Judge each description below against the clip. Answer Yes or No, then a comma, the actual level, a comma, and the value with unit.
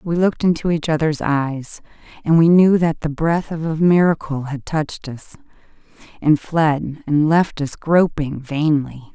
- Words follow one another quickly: No, average, 165 wpm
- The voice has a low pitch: No, medium, 155 Hz